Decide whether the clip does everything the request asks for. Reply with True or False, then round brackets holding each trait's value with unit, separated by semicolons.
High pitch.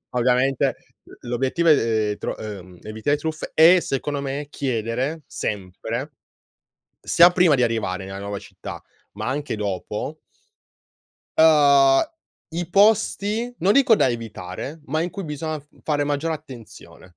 False (140 Hz)